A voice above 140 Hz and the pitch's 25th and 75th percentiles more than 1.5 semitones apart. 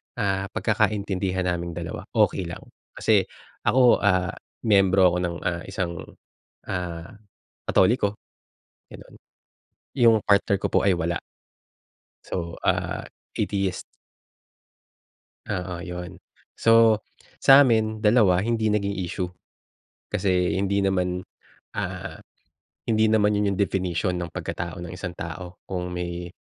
No: very low, 95 Hz; average, 2.9 semitones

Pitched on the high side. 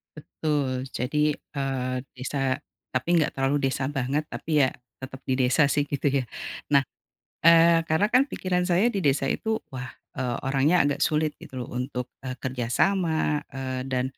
No: medium, 140 Hz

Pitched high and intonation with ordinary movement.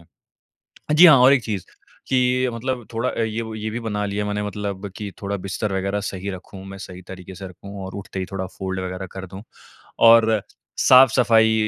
No: low, 105 Hz; average, 3.1 semitones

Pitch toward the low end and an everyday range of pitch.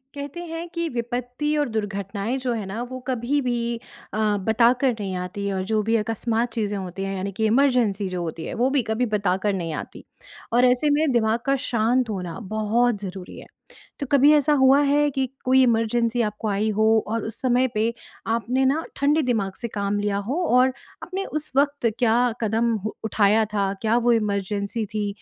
No: high, 230 Hz; average, 3.8 semitones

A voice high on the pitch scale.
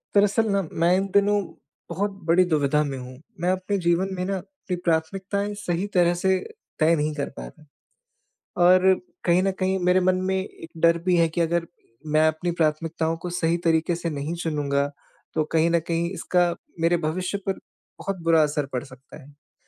No: medium, 170 Hz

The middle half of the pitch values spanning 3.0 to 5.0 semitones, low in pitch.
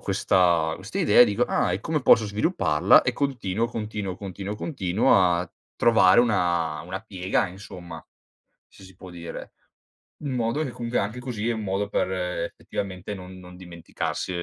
Yes: average, 3.9 semitones; very low, 95 Hz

